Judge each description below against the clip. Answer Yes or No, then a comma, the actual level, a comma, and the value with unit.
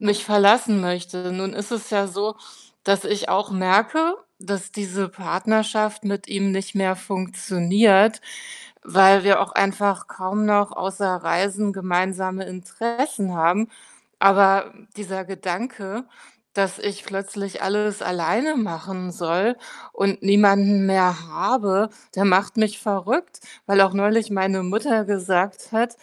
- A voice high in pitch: Yes, high, 195 Hz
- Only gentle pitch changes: Yes, narrow, 1.9 semitones